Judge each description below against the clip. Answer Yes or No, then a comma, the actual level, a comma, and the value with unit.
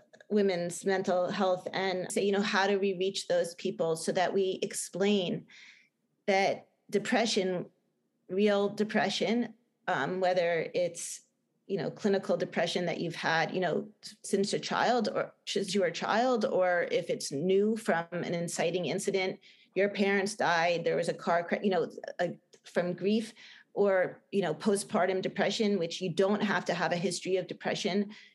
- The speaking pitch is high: Yes, high, 195 Hz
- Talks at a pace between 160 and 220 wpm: Yes, average, 165 wpm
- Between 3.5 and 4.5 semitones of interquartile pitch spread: No, narrow, 2.4 semitones